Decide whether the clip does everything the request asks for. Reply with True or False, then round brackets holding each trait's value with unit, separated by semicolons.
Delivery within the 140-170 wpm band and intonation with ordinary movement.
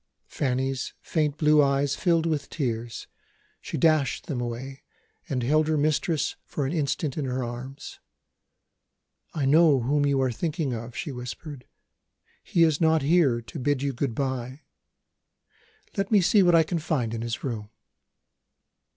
True (155 wpm; 3.7 semitones)